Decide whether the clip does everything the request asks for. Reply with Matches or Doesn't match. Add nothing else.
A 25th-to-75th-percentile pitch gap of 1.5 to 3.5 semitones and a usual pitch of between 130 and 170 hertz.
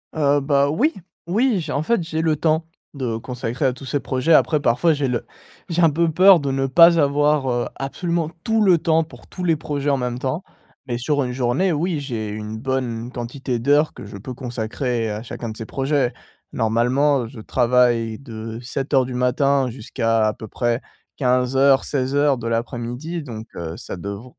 Doesn't match